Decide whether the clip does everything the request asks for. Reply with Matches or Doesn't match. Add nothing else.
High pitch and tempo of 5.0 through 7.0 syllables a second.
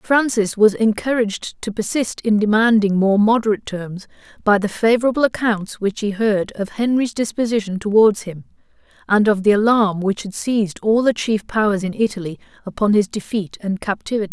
Matches